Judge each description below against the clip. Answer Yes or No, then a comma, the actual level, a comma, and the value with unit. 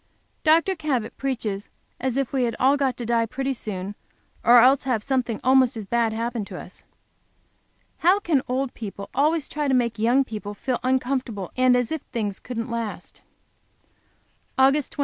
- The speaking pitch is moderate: No, very high, 250 Hz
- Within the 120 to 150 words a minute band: No, average, 170 wpm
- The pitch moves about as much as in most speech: Yes, average, 3.0 semitones